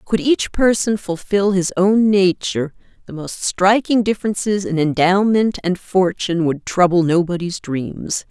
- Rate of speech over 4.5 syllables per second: No, 4.4 syllables/s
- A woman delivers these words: Yes, female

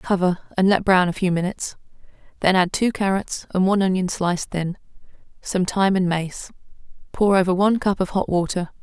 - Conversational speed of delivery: Yes, average, 185 wpm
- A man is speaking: No, female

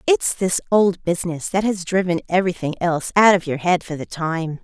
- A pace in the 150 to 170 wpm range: No, fast, 205 wpm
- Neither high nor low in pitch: Yes, medium, 180 Hz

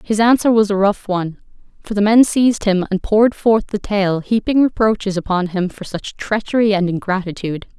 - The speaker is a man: No, female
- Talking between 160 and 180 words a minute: No, average, 195 wpm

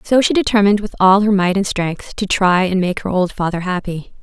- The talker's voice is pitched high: Yes, high, 195 Hz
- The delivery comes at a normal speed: No, fast, 240 wpm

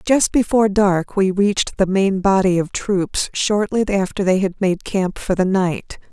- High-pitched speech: Yes, high, 195 Hz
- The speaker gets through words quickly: No, average, 185 wpm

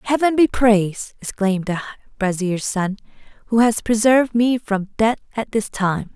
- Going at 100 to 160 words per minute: Yes, average, 155 wpm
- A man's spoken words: No, female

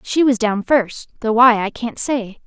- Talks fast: Yes, fast, 220 wpm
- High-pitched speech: Yes, high, 230 Hz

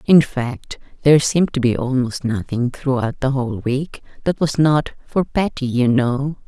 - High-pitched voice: No, low, 135 Hz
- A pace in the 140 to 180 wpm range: Yes, average, 175 wpm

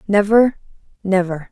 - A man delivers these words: No, female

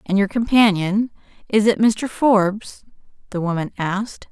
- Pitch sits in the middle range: No, high, 205 Hz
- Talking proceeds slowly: Yes, slow, 125 wpm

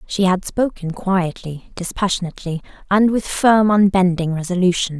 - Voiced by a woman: Yes, female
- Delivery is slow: Yes, slow, 120 wpm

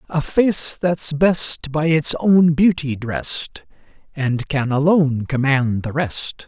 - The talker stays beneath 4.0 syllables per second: Yes, 3.3 syllables/s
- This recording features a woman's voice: No, male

